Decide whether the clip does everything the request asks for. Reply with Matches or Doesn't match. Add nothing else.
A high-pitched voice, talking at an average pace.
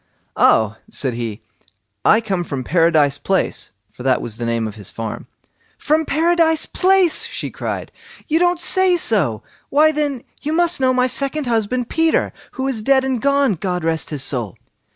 Matches